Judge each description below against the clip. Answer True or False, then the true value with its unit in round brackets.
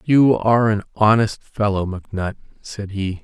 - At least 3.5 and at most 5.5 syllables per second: True (4.9 syllables/s)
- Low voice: True (105 Hz)